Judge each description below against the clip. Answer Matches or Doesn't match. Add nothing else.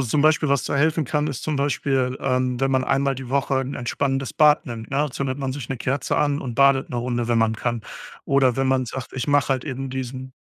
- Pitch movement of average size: Doesn't match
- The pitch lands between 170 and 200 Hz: Doesn't match